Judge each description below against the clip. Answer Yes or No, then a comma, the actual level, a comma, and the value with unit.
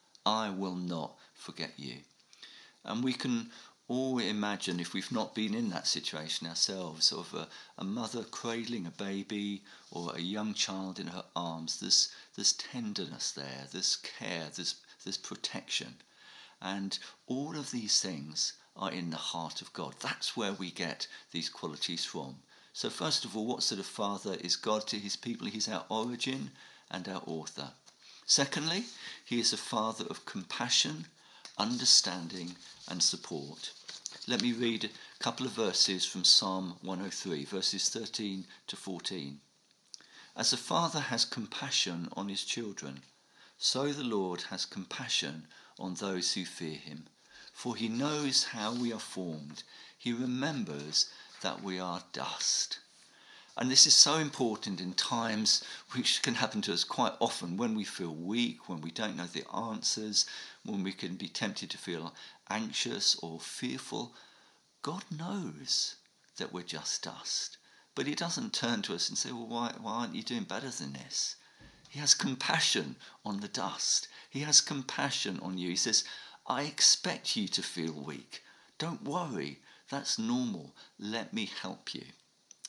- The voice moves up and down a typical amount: No, wide, 5.8 semitones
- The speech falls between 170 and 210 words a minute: No, average, 155 wpm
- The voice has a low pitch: Yes, low, 100 Hz